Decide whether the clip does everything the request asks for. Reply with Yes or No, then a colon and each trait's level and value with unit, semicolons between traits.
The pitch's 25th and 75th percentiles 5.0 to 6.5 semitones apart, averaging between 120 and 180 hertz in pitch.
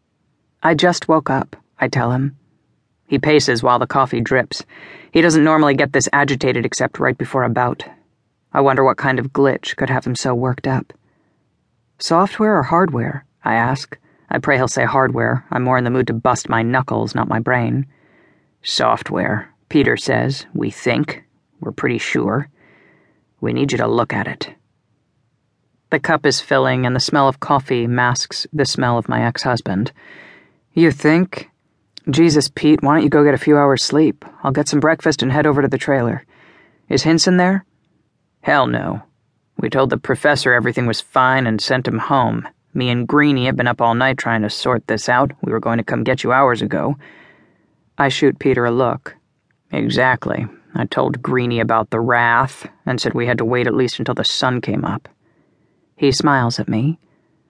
No: average, 3.2 semitones; low, 135 Hz